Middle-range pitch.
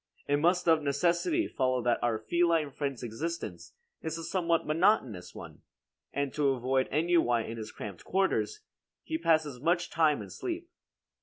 Yes: medium, 155 Hz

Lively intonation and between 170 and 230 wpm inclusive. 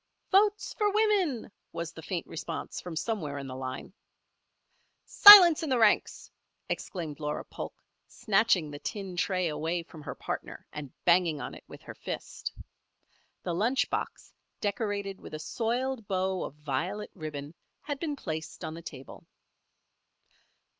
No: wide, 7.0 semitones; average, 145 wpm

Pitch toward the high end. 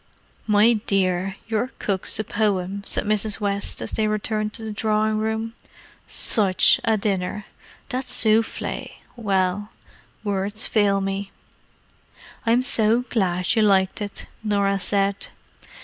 Yes: high, 210 Hz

